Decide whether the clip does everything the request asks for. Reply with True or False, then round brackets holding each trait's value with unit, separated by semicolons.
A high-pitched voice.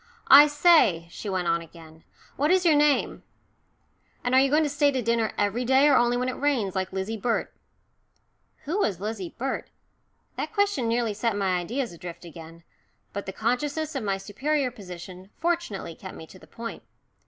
True (230 Hz)